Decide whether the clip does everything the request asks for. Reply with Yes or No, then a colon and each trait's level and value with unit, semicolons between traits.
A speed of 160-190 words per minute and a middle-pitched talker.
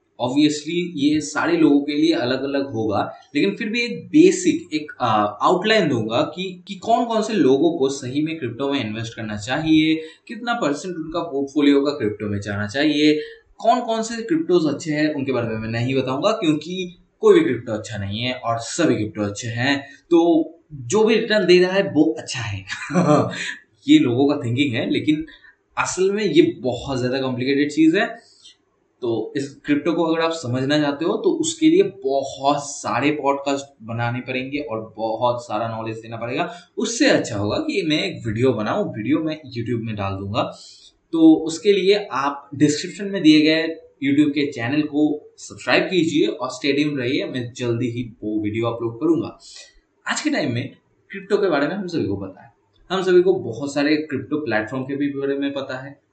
Yes: average, 185 wpm; medium, 150 Hz